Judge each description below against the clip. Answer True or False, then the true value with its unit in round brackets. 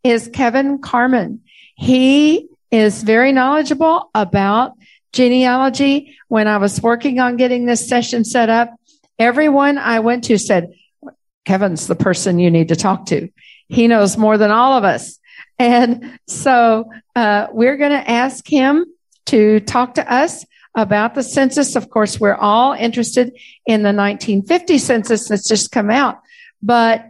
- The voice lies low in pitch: False (240 Hz)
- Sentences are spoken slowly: False (150 wpm)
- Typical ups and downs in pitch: True (3.7 semitones)